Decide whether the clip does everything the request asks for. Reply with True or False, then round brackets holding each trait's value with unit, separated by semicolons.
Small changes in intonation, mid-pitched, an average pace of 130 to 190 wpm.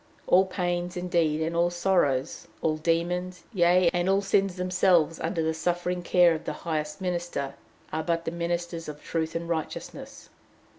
True (1.7 semitones; 170 Hz; 160 wpm)